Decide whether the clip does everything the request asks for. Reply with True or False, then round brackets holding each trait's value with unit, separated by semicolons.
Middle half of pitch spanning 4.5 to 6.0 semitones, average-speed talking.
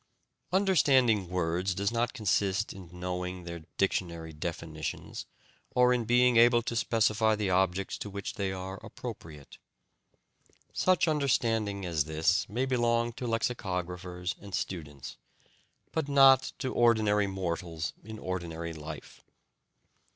False (5.0 semitones; 120 wpm)